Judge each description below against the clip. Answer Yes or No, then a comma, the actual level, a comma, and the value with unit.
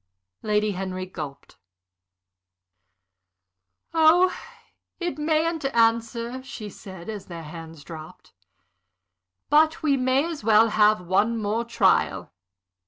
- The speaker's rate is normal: No, slow, 105 wpm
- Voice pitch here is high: Yes, high, 225 Hz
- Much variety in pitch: Yes, wide, 6.8 semitones